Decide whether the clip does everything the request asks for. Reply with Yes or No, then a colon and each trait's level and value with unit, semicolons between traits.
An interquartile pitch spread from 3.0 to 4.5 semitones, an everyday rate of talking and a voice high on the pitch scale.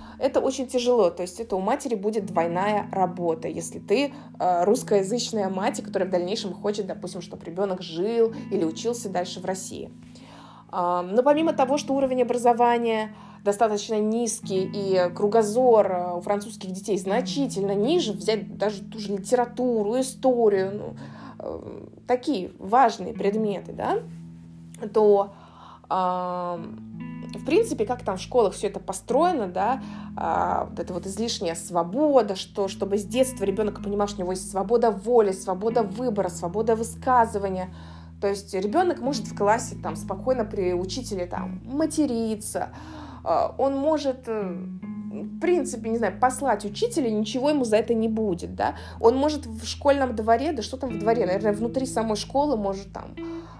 Yes: average, 4.2 semitones; average, 145 wpm; high, 210 Hz